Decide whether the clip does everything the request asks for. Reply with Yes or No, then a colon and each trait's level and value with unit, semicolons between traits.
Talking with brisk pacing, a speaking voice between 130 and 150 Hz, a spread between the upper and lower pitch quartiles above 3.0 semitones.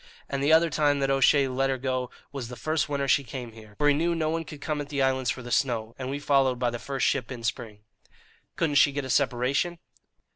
No: fast, 250 wpm; low, 135 Hz; narrow, 2.6 semitones